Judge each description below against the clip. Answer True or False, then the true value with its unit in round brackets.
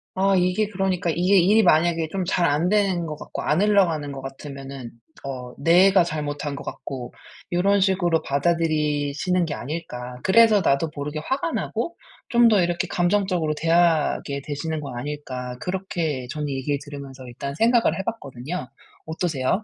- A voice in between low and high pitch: True (165 Hz)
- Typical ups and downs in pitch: True (4.8 semitones)